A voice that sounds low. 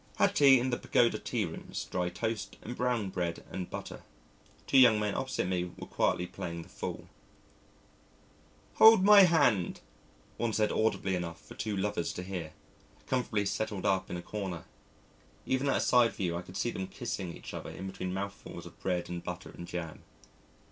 Yes: low, 100 Hz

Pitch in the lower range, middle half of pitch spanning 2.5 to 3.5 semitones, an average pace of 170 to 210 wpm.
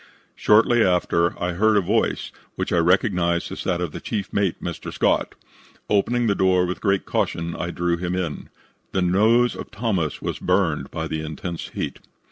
Yes: very low, 90 Hz; average, 3.1 semitones; average, 180 wpm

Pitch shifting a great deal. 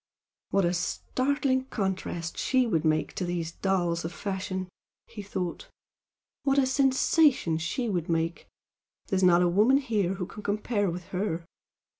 Yes: wide, 5.9 semitones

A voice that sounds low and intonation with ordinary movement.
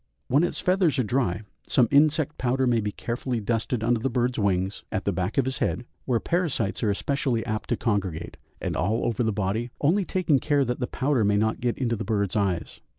Yes: low, 120 Hz; average, 4.5 semitones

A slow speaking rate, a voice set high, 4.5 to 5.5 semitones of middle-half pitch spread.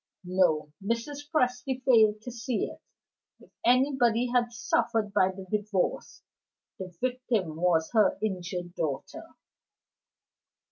Yes: slow, 110 wpm; high, 220 Hz; average, 5.1 semitones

